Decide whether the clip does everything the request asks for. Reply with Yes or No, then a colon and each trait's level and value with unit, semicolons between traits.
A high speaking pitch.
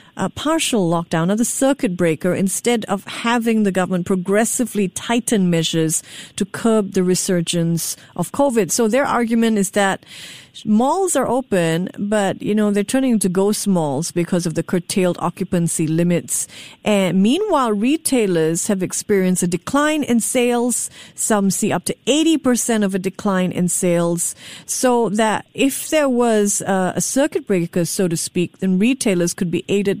Yes: high, 200 Hz